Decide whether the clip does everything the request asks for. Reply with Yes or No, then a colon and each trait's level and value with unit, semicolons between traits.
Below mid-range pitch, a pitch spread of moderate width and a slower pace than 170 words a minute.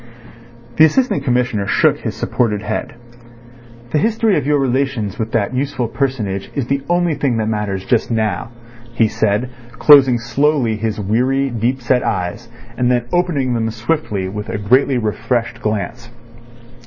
Yes: low, 120 Hz; average, 4.0 semitones; average, 155 wpm